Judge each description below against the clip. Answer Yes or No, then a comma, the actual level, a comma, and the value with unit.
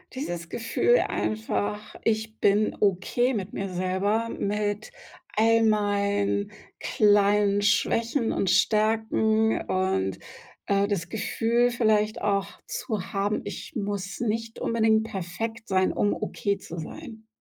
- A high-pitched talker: Yes, high, 210 Hz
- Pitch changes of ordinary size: No, narrow, 2.0 semitones